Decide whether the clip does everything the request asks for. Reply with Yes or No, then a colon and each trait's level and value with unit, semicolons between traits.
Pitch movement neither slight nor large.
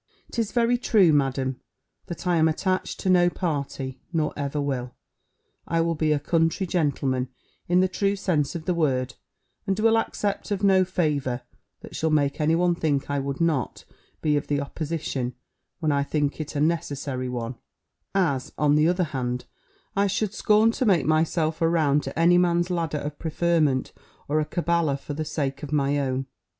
Yes: average, 3.8 semitones